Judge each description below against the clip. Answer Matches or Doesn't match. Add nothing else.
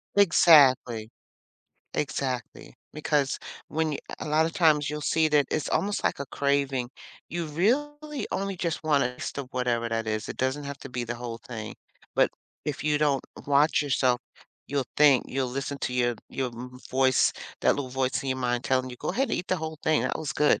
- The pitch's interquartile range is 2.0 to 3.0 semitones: Doesn't match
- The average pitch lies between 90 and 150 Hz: Matches